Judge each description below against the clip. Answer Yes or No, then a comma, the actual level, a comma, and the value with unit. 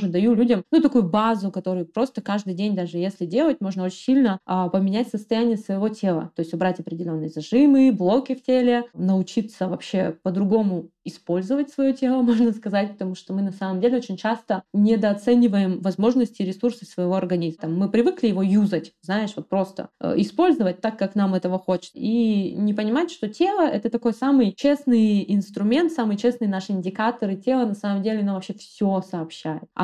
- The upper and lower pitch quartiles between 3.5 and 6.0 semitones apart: Yes, average, 4.0 semitones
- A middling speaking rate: No, fast, 170 wpm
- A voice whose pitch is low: No, high, 205 Hz